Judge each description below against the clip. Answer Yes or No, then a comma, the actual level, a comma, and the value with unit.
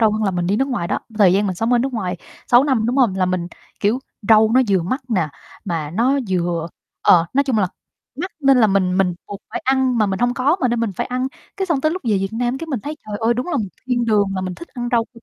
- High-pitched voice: Yes, high, 225 Hz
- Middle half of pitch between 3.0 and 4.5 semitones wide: No, average, 5.0 semitones